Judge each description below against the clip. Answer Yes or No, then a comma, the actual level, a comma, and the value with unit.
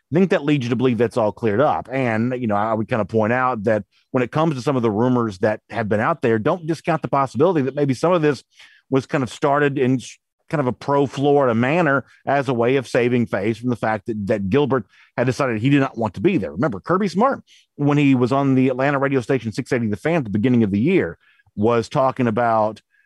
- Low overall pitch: Yes, low, 130 Hz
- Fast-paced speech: Yes, fast, 250 wpm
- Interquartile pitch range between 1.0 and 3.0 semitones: No, average, 3.7 semitones